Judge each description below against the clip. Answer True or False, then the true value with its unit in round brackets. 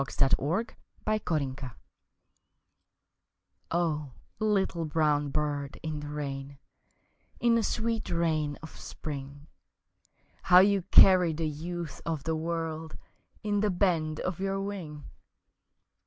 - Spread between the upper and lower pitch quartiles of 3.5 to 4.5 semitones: True (4.1 semitones)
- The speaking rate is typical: False (110 wpm)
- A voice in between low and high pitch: True (160 Hz)